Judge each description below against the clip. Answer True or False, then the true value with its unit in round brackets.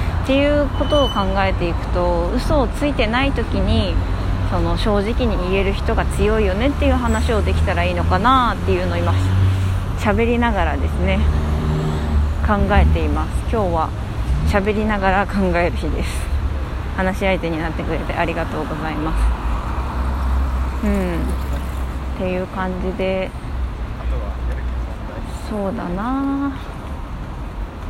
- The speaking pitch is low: True (80 Hz)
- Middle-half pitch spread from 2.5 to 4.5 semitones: False (5.2 semitones)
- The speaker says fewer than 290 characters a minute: True (265 characters per minute)